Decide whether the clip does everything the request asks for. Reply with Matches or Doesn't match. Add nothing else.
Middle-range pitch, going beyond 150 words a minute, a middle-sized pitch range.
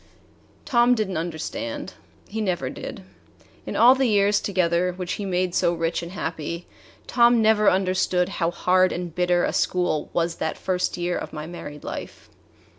Matches